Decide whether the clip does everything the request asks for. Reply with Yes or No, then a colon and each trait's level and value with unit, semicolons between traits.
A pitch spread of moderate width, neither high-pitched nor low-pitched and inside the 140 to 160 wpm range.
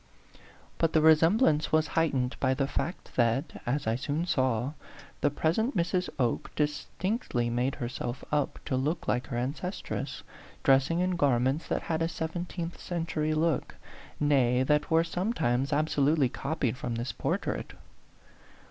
Yes: average, 4.2 semitones; medium, 150 Hz; average, 150 wpm